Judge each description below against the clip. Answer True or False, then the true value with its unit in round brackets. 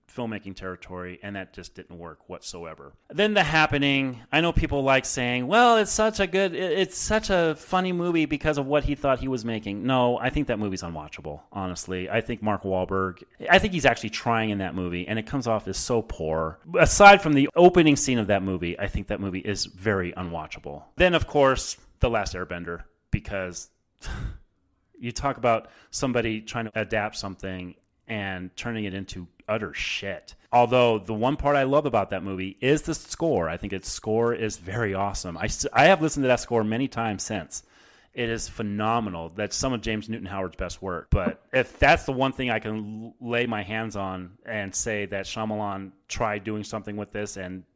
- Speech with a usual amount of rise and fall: False (5.8 semitones)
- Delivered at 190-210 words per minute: True (200 wpm)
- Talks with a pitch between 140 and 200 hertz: False (110 Hz)